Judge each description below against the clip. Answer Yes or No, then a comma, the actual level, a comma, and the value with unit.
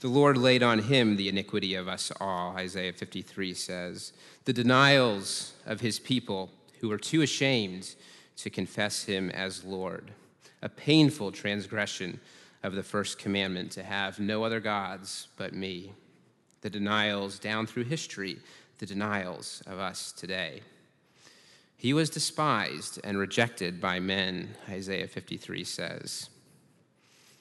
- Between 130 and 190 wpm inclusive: Yes, slow, 135 wpm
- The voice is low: Yes, low, 100 Hz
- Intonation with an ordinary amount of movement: Yes, average, 3.7 semitones